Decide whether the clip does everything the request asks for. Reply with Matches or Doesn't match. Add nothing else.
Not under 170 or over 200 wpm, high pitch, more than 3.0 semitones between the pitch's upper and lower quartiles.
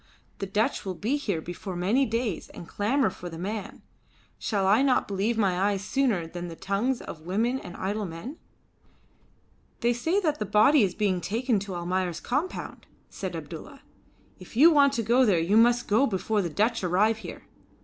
Matches